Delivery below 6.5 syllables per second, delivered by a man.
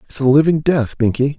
Yes: 5.4 syllables/s; male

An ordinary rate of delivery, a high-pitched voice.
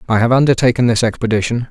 No: average, 175 wpm; low, 120 Hz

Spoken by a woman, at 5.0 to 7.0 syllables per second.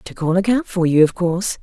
Yes: female; 5.7 syllables/s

